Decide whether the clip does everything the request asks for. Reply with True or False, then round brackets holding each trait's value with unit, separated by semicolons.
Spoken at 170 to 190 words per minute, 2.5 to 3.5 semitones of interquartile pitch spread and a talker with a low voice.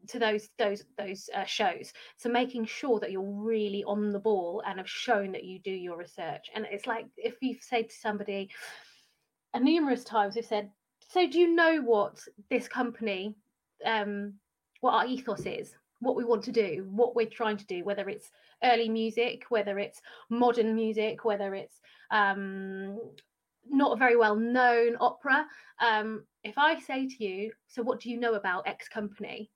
False (180 wpm; 3.0 semitones; 220 Hz)